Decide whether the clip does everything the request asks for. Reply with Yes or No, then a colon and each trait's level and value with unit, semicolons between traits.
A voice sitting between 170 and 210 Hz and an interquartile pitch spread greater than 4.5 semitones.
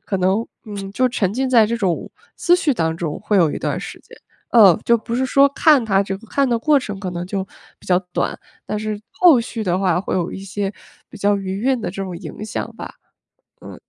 No: high, 205 Hz; average, 3.9 semitones